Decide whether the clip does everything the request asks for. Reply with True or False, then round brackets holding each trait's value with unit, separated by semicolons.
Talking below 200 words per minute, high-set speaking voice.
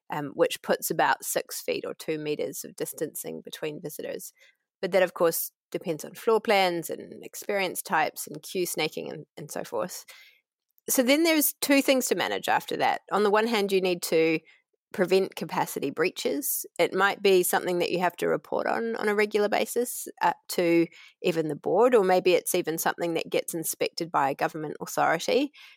True (190 wpm; 210 Hz)